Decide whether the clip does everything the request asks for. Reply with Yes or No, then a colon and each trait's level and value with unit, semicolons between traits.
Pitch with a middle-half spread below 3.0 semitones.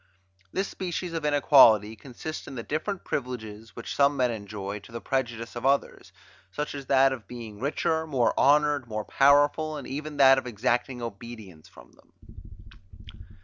No: average, 4.0 semitones